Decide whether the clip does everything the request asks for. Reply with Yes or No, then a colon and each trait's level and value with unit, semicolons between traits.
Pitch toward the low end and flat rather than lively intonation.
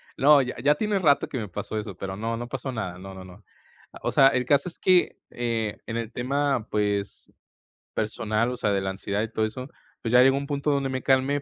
No: low, 120 Hz; average, 4.6 semitones